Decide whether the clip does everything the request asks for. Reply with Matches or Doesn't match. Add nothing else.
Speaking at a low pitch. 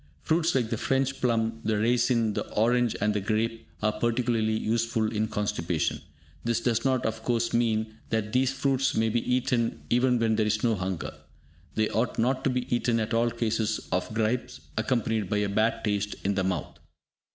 Matches